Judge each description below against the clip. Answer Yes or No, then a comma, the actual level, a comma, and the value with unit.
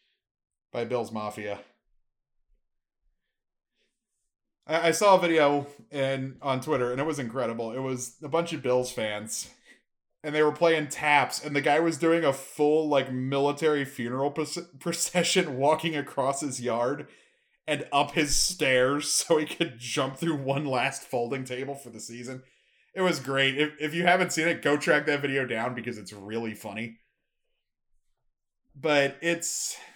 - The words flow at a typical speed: Yes, average, 155 wpm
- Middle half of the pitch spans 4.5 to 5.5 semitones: No, average, 3.9 semitones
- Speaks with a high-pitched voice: No, medium, 140 Hz